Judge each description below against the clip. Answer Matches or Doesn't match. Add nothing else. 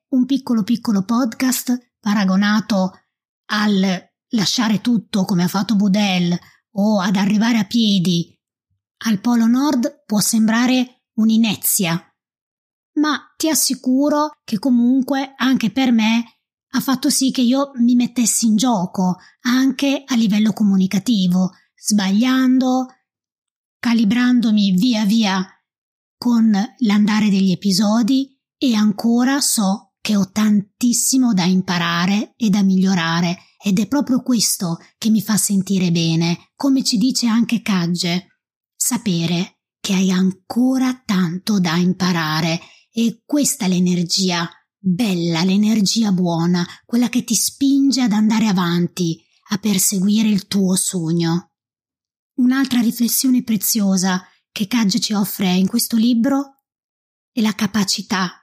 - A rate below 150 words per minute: Matches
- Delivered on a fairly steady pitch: Doesn't match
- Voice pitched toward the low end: Doesn't match